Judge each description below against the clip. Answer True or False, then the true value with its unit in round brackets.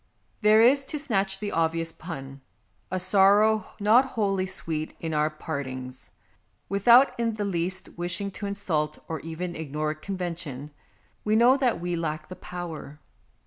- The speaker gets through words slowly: False (150 wpm)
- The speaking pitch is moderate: True (180 Hz)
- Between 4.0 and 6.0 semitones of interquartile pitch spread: True (4.6 semitones)